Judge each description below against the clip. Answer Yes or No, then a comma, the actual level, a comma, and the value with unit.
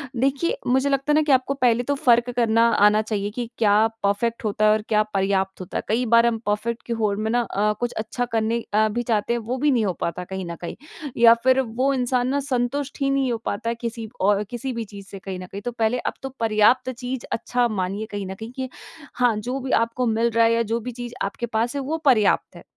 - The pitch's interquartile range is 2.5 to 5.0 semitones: Yes, average, 2.8 semitones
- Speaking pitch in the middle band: No, high, 230 Hz